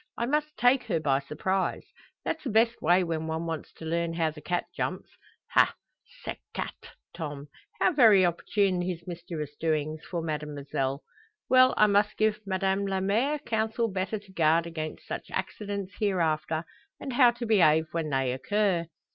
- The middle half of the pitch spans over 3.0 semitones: Yes, average, 5.1 semitones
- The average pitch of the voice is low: No, medium, 180 Hz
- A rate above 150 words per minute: Yes, average, 165 wpm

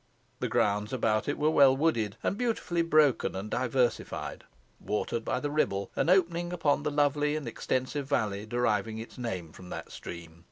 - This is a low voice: Yes, low, 130 Hz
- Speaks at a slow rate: No, average, 170 wpm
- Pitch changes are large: Yes, wide, 5.9 semitones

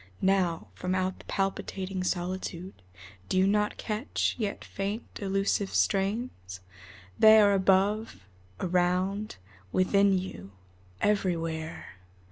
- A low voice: No, high, 190 Hz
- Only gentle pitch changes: Yes, narrow, 1.8 semitones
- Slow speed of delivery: Yes, slow, 100 wpm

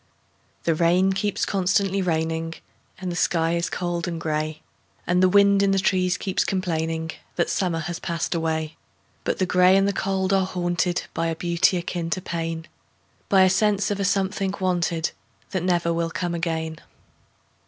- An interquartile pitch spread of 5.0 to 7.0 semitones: No, narrow, 2.4 semitones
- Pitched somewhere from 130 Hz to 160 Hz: No, medium, 175 Hz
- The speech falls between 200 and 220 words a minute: No, average, 150 wpm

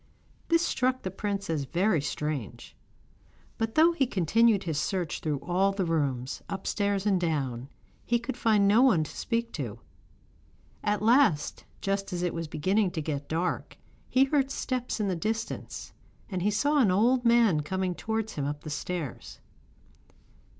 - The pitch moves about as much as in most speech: No, wide, 6.2 semitones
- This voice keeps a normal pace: Yes, average, 165 wpm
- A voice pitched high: Yes, high, 195 Hz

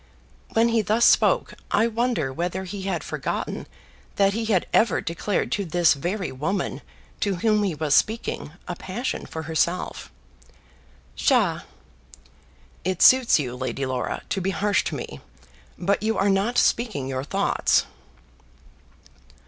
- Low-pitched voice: No, high, 190 Hz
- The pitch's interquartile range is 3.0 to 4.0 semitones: No, average, 4.9 semitones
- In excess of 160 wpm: No, average, 140 wpm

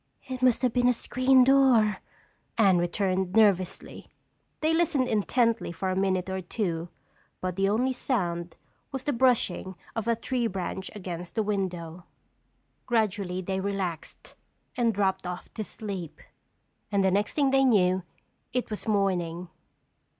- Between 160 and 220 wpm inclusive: No, average, 145 wpm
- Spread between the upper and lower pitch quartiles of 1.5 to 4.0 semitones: No, average, 4.7 semitones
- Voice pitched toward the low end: No, high, 200 Hz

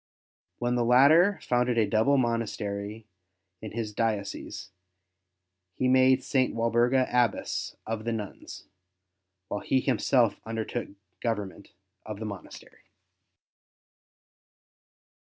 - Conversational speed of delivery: No, slow, 110 wpm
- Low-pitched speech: Yes, low, 115 Hz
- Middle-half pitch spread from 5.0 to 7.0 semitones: No, average, 2.8 semitones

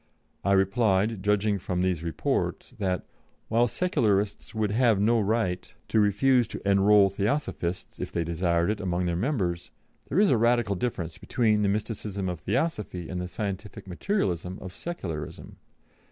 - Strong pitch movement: No, average, 3.6 semitones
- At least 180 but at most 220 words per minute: No, average, 155 wpm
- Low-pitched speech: Yes, low, 100 Hz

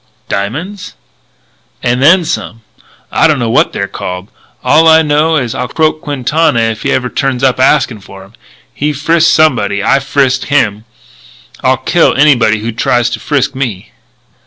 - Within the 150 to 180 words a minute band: Yes, average, 160 wpm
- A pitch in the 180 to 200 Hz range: No, low, 130 Hz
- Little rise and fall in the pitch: No, average, 5.1 semitones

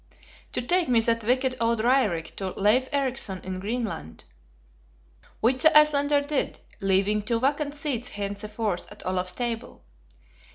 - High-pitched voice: Yes, high, 230 Hz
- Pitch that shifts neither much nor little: Yes, average, 4.9 semitones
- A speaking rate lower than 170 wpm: Yes, slow, 135 wpm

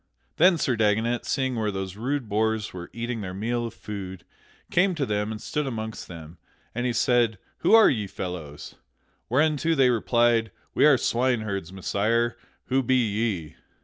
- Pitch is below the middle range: Yes, low, 115 Hz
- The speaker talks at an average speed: Yes, average, 165 wpm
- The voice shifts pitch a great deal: No, average, 3.7 semitones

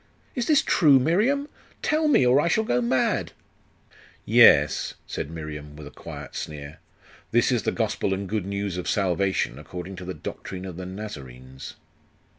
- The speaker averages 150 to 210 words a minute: Yes, average, 165 wpm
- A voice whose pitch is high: No, very low, 95 Hz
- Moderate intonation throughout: No, wide, 9.0 semitones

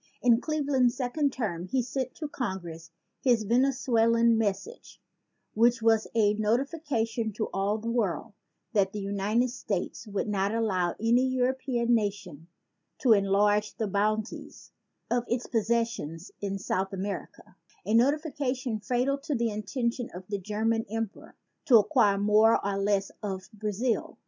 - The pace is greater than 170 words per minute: No, average, 140 wpm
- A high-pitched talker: Yes, high, 225 Hz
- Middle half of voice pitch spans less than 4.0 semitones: Yes, average, 3.4 semitones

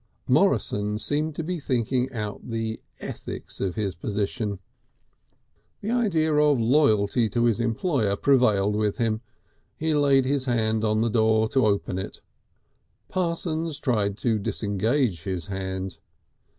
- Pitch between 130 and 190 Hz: No, low, 115 Hz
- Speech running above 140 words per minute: No, slow, 135 wpm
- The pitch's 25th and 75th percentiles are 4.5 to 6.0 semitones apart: Yes, wide, 5.5 semitones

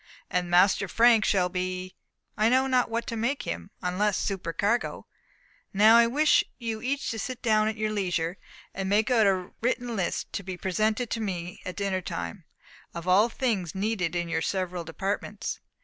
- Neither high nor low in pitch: No, high, 200 Hz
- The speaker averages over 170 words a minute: Yes, average, 180 wpm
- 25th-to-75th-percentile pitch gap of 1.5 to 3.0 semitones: No, average, 3.9 semitones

